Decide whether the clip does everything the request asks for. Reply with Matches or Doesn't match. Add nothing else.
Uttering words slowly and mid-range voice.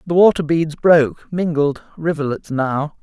Matches